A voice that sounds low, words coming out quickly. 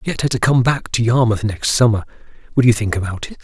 Yes: low, 115 Hz; fast, 280 wpm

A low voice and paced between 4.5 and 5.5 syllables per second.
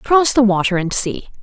No: high, 220 Hz; 5.0 syllables/s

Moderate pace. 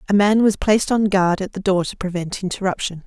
No: fast, 235 wpm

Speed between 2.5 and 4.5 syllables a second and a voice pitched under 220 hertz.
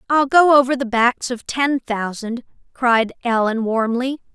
No: 4.1 syllables/s; high, 245 Hz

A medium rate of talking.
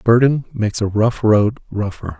Yes: average, 190 wpm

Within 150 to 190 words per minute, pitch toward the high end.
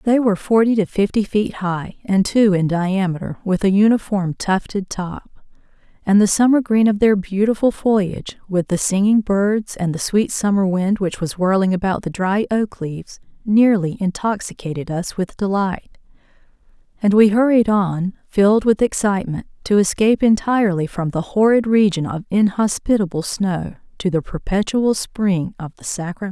Yes: average, 160 wpm; high, 200 Hz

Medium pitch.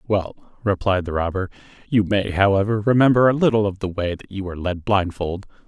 No: low, 100 Hz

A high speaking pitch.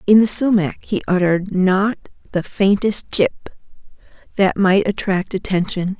Yes: high, 195 Hz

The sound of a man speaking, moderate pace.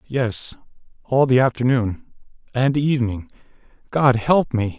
No: male; slow, 75 wpm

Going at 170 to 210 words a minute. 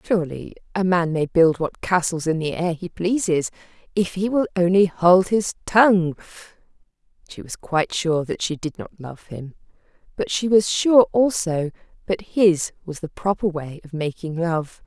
Yes: average, 175 wpm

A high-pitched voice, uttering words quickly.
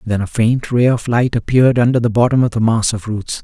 No: low, 115 Hz; fast, 260 wpm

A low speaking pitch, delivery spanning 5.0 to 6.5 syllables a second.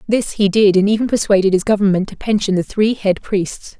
No: high, 200 Hz; 5.5 syllables/s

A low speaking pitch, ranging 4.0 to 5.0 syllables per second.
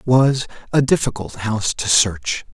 Yes: low, 120 Hz; 4.6 syllables/s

